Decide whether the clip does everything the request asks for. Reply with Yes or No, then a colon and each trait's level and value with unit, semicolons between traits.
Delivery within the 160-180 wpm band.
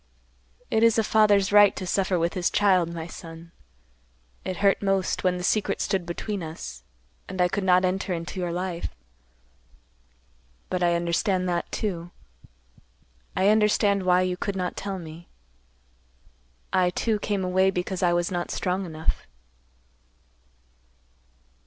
No: average, 145 wpm